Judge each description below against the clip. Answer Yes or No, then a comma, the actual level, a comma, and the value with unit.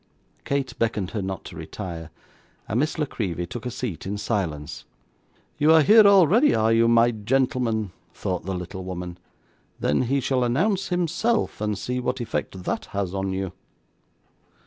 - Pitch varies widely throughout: Yes, wide, 6.2 semitones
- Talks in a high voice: No, low, 115 Hz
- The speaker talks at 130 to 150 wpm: No, average, 165 wpm